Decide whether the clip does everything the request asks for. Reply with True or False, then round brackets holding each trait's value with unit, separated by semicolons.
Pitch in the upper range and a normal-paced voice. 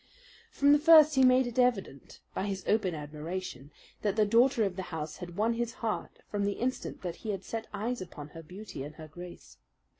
False (200 Hz; 210 wpm)